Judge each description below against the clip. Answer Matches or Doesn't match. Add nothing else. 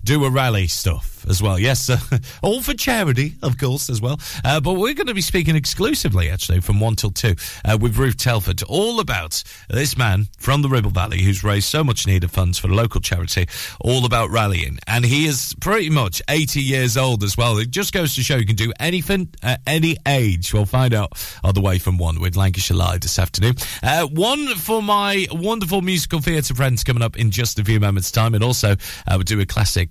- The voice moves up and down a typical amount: Doesn't match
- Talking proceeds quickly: Matches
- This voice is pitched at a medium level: Doesn't match